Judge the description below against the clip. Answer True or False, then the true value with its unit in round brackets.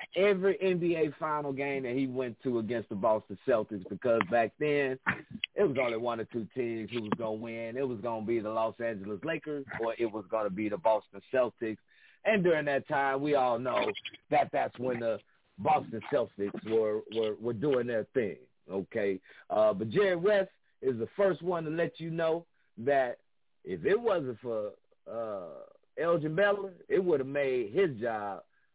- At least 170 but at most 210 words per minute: True (190 wpm)